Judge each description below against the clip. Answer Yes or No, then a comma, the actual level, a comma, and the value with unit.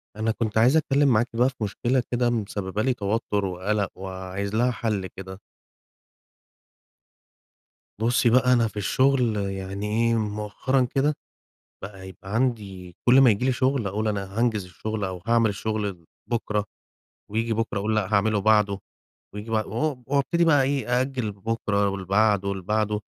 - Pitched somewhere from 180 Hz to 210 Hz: No, low, 110 Hz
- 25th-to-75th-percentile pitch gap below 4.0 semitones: Yes, average, 3.4 semitones